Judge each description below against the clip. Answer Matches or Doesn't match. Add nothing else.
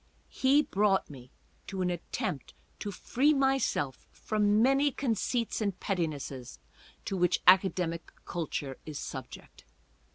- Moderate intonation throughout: Doesn't match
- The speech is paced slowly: Matches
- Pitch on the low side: Doesn't match